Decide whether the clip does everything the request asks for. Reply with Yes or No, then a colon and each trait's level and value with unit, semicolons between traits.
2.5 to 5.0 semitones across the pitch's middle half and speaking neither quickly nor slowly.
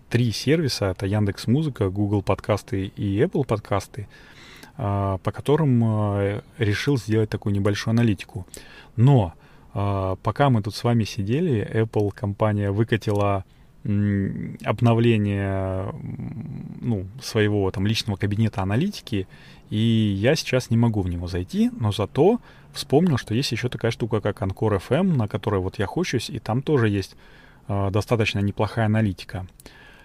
Yes: average, 3.2 semitones; average, 130 wpm